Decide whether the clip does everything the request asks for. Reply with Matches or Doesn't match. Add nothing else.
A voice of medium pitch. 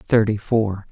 Doesn't match